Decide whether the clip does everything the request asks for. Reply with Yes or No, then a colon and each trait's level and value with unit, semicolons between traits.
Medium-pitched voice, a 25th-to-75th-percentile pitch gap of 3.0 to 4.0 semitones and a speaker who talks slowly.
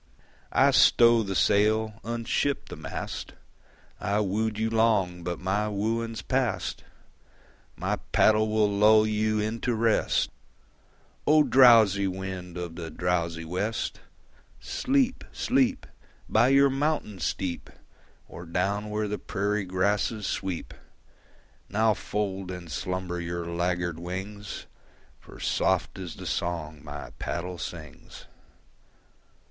No: low, 100 Hz; average, 3.6 semitones; slow, 115 wpm